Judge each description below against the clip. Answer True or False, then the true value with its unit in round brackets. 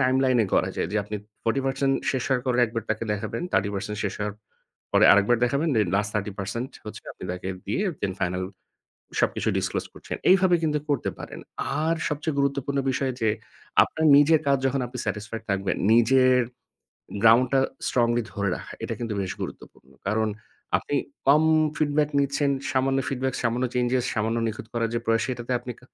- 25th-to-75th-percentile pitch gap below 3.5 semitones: False (4.1 semitones)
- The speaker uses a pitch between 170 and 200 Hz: False (125 Hz)